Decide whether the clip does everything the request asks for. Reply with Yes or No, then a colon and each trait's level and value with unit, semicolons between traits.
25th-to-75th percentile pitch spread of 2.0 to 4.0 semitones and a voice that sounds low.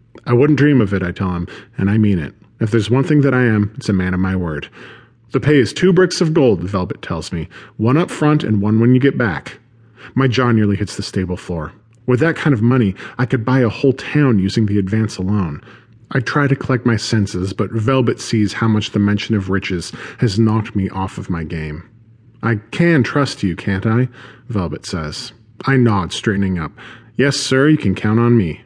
No: average, 4.8 semitones; low, 115 Hz